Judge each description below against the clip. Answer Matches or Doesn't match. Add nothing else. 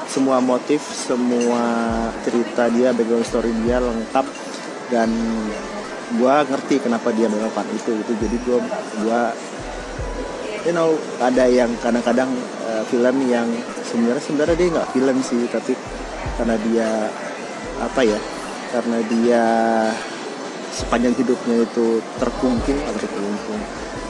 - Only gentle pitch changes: Matches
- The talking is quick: Doesn't match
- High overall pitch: Doesn't match